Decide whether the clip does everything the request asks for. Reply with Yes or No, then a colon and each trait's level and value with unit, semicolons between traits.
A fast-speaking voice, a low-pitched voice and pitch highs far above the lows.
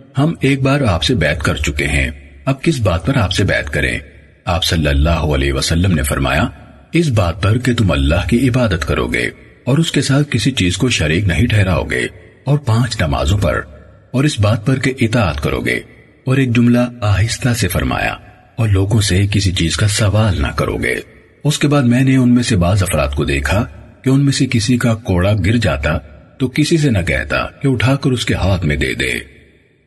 Yes: fast, 215 wpm; low, 105 Hz; wide, 7.6 semitones